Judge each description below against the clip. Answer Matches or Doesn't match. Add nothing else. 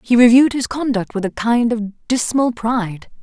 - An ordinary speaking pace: Matches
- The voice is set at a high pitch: Matches